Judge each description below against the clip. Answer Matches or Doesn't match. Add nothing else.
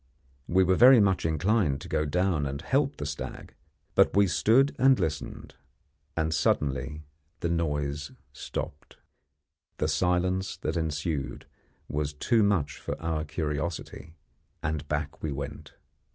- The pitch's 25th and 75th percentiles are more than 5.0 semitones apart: Doesn't match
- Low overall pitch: Matches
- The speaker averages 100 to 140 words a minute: Matches